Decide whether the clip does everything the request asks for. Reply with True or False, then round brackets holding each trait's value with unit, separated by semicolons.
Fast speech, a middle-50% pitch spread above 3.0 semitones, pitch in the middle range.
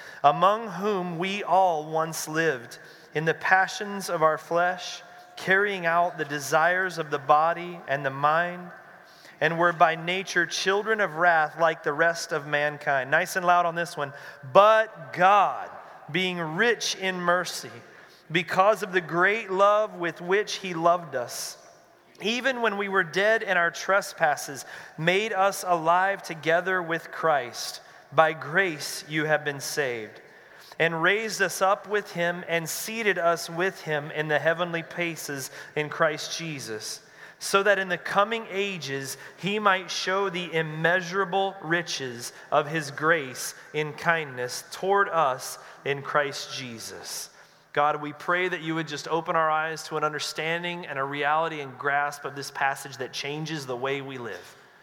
False (155 wpm; 3.8 semitones; 170 Hz)